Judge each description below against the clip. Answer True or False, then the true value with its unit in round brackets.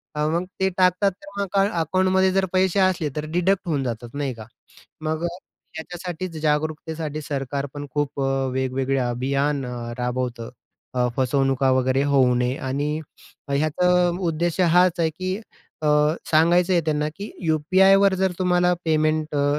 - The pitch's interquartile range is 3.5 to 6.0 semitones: True (4.7 semitones)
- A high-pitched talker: False (155 Hz)